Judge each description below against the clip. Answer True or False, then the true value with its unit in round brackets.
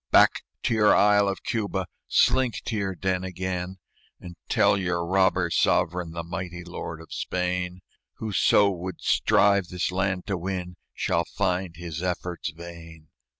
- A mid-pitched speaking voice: False (90 Hz)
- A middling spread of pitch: False (1.9 semitones)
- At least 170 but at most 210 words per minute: False (150 wpm)